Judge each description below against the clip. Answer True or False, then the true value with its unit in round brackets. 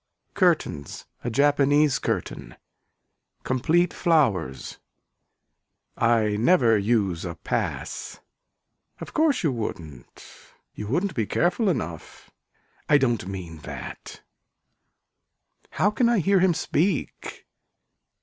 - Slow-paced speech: True (100 wpm)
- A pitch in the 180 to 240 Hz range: False (125 Hz)